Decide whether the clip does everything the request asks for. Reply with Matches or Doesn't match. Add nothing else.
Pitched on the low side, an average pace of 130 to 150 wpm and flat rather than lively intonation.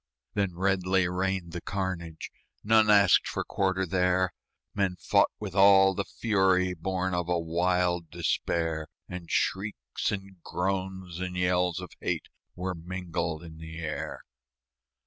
Matches